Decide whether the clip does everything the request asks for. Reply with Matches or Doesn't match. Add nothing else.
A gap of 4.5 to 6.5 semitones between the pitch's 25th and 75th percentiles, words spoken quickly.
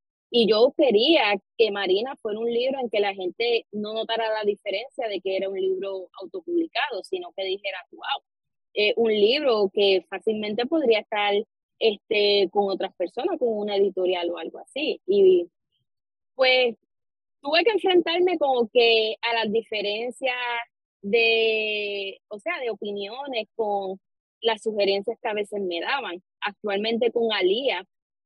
Doesn't match